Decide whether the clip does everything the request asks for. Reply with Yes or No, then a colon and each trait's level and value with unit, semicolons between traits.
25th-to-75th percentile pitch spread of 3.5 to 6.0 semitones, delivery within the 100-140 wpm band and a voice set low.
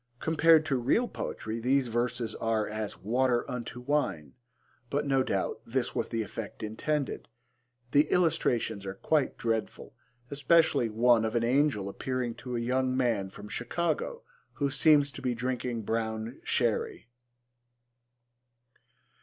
Yes: average, 4.1 semitones; slow, 135 wpm; low, 125 Hz